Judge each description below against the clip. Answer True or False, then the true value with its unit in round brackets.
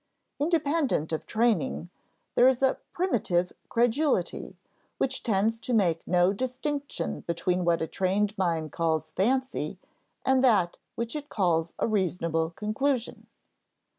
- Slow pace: True (125 wpm)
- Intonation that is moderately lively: False (7.0 semitones)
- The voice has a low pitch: False (210 Hz)